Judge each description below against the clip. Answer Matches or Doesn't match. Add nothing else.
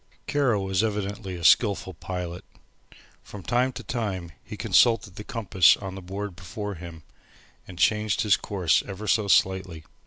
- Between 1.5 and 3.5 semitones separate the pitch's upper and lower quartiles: Matches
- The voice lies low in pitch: Matches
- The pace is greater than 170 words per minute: Doesn't match